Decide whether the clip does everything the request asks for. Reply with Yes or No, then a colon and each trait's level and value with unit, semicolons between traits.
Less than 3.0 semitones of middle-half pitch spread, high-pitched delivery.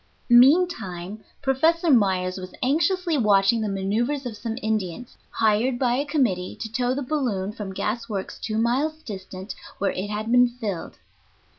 No: average, 5.2 semitones; high, 225 Hz